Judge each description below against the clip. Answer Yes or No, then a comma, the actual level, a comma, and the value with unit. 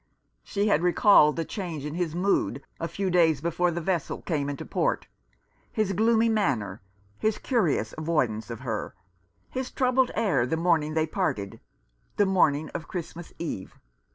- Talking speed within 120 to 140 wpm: No, average, 160 wpm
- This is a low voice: No, medium, 165 Hz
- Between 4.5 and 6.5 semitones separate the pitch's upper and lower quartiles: Yes, average, 5.2 semitones